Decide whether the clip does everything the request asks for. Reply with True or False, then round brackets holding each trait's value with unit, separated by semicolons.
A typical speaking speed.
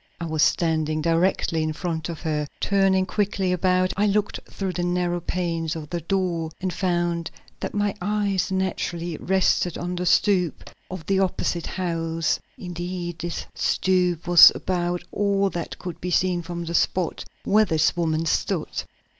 True (160 wpm)